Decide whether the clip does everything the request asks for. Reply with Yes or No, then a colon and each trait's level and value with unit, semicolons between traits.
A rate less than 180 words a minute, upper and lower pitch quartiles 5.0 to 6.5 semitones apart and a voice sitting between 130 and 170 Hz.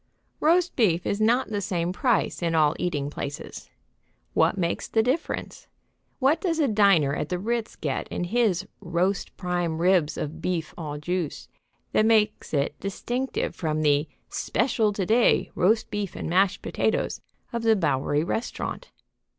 No: average, 155 wpm; wide, 5.5 semitones; medium, 185 Hz